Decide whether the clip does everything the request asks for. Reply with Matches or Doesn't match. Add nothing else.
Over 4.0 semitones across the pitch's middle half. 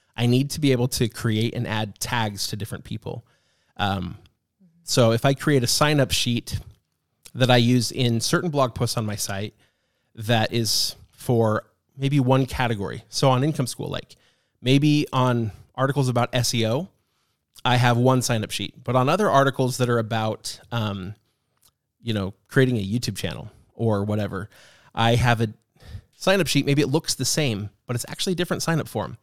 Doesn't match